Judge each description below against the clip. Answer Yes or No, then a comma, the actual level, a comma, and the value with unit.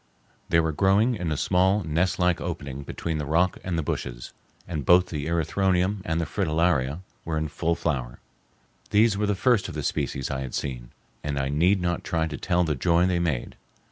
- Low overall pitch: Yes, very low, 85 Hz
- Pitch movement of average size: Yes, average, 3.6 semitones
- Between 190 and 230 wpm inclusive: Yes, average, 200 wpm